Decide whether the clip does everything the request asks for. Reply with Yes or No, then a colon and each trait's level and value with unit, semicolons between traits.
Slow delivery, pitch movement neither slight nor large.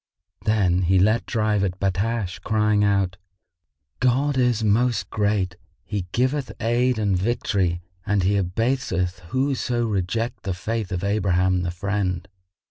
Yes: slow, 130 wpm; average, 3.9 semitones